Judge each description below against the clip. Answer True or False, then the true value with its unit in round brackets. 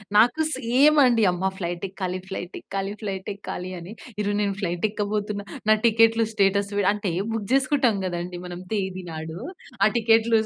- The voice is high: True (205 Hz)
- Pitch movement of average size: True (3.4 semitones)